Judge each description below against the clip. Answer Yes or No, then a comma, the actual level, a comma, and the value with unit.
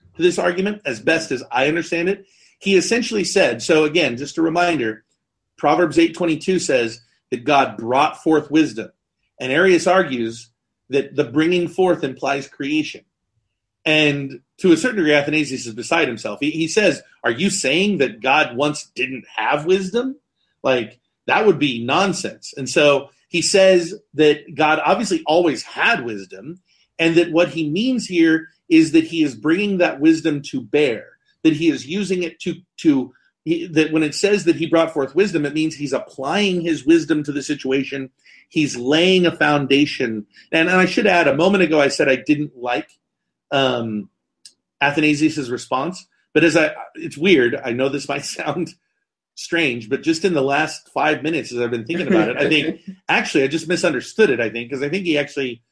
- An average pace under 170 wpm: No, average, 180 wpm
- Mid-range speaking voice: Yes, medium, 160 Hz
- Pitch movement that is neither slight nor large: Yes, average, 4.6 semitones